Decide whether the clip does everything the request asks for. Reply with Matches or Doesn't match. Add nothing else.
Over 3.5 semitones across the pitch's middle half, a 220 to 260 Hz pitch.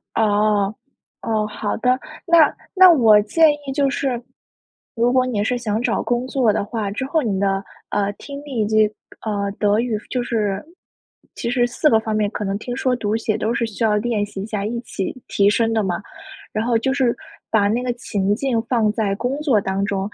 Doesn't match